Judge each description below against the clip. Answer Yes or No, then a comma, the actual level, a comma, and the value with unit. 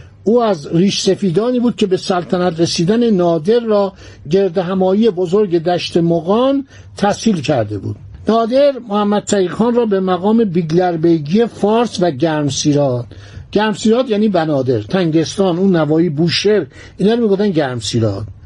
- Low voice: No, medium, 185 Hz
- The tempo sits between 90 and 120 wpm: No, average, 130 wpm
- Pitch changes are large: No, average, 4.4 semitones